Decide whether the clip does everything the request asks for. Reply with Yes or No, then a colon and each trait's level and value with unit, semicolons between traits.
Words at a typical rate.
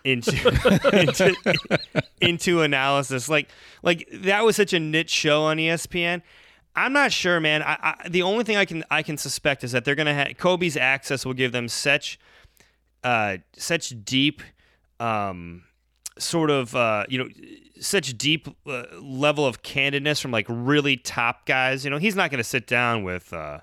Yes: average, 175 wpm